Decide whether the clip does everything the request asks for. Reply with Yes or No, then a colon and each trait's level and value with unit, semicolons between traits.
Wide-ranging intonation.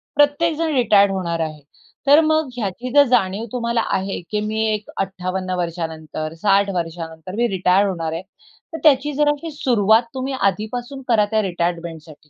Yes: wide, 6.4 semitones